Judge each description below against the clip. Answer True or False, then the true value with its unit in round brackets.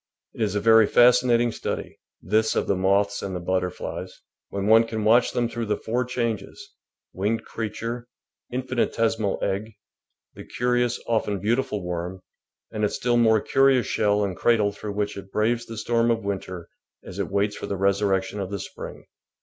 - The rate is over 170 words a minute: True (180 wpm)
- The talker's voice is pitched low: True (105 Hz)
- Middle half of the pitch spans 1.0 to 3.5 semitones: True (2.9 semitones)